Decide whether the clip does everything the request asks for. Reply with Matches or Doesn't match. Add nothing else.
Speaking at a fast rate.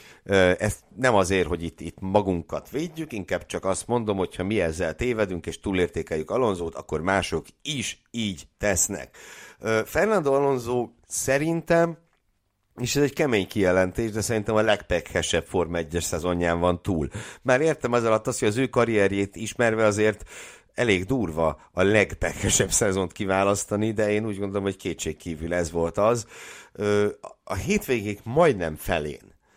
Doesn't match